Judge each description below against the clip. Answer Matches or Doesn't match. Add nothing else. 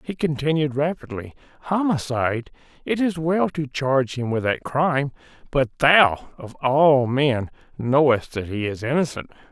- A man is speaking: Matches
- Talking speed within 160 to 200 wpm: Doesn't match